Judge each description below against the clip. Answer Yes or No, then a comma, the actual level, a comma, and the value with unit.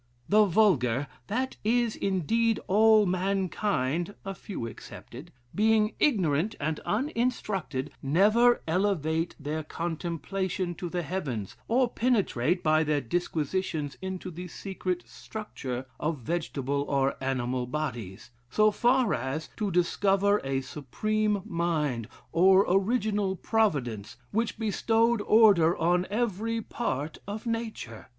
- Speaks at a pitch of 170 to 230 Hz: Yes, medium, 185 Hz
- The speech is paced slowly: Yes, slow, 115 wpm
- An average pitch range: No, wide, 6.2 semitones